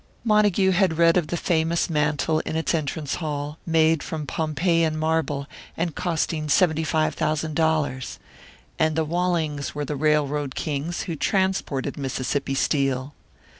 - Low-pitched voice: No, medium, 155 Hz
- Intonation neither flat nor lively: No, narrow, 2.2 semitones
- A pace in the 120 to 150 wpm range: Yes, average, 140 wpm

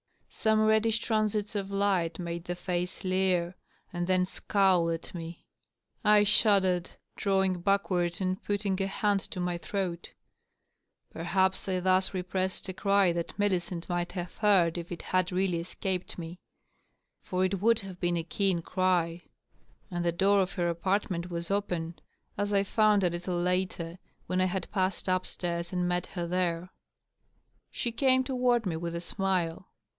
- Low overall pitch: No, medium, 185 Hz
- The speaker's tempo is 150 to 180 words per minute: Yes, average, 165 wpm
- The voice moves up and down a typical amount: No, narrow, 2.2 semitones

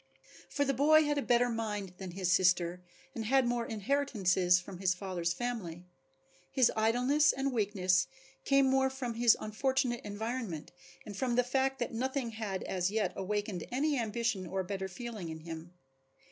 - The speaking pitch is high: Yes, high, 220 Hz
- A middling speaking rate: Yes, average, 165 wpm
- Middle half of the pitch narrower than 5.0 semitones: No, wide, 5.4 semitones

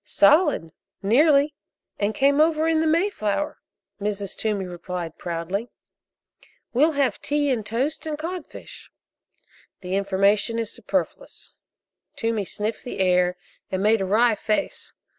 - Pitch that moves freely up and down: Yes, wide, 7.0 semitones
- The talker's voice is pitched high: Yes, high, 225 Hz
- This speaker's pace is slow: Yes, slow, 125 wpm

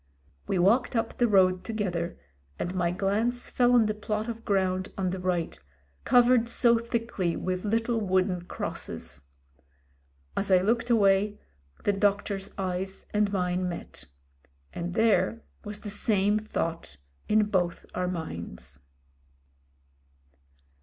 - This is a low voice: No, high, 195 Hz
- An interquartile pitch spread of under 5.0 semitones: Yes, average, 3.4 semitones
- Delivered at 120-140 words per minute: Yes, slow, 135 wpm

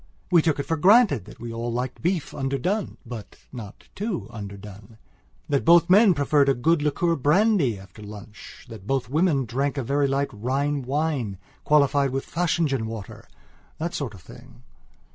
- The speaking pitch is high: No, low, 135 Hz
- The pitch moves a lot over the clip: Yes, wide, 5.9 semitones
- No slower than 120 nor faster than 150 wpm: No, average, 160 wpm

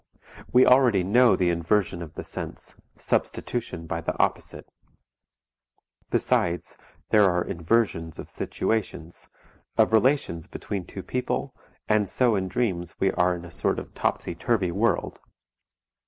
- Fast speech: No, slow, 135 wpm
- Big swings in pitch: No, average, 4.7 semitones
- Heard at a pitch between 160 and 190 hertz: No, very low, 95 Hz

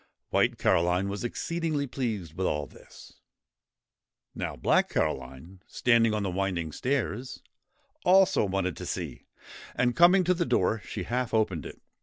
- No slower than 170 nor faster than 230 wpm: No, average, 145 wpm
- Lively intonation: Yes, wide, 6.2 semitones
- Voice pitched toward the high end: No, low, 105 Hz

